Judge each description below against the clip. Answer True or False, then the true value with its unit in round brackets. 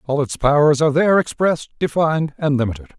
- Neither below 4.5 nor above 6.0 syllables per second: False (6.8 syllables/s)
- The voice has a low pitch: False (145 Hz)